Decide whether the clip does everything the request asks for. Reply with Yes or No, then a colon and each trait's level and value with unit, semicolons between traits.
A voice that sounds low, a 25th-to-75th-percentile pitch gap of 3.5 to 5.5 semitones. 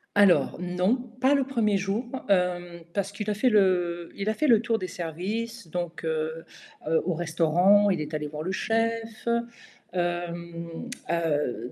No: medium, 180 Hz; average, 4.3 semitones